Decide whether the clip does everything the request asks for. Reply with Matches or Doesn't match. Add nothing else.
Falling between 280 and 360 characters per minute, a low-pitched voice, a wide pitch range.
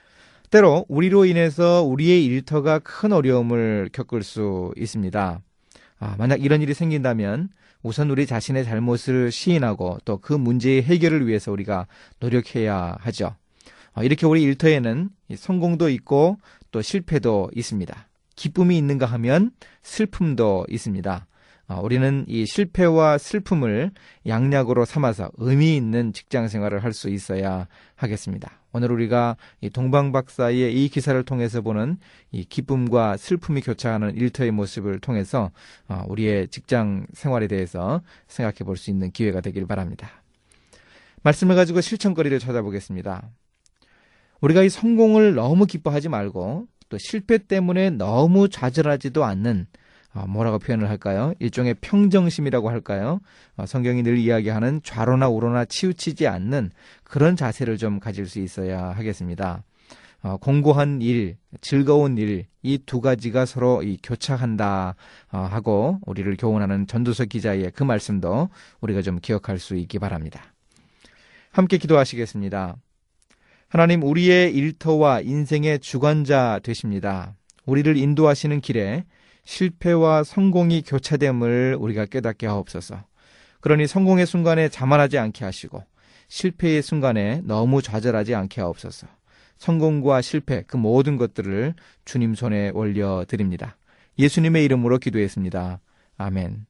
Matches